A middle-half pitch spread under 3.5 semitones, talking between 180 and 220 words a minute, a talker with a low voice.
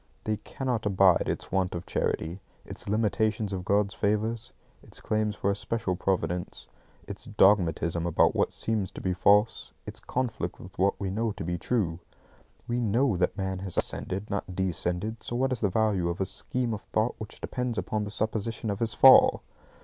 Yes: average, 3.0 semitones; average, 185 wpm; low, 105 Hz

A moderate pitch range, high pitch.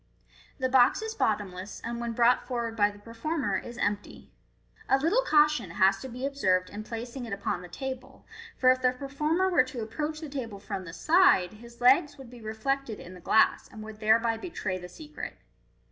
Yes: average, 4.6 semitones; high, 235 Hz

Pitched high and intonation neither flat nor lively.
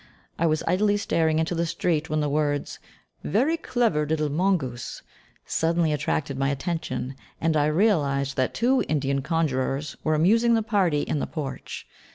No: medium, 155 Hz; average, 3.8 semitones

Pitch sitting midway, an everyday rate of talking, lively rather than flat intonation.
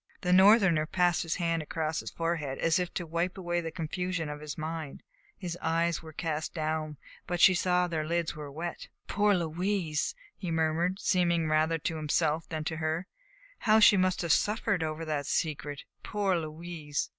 No: medium, 165 Hz; average, 180 wpm; narrow, 2.4 semitones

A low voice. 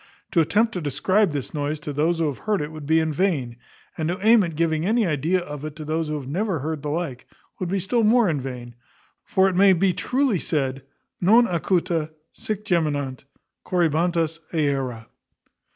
No: medium, 165 Hz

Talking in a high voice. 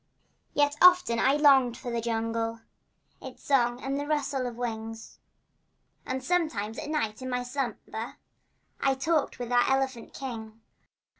Yes: very high, 250 Hz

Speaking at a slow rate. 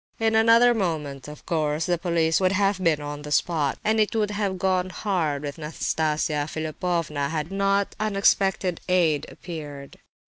No: average, 160 wpm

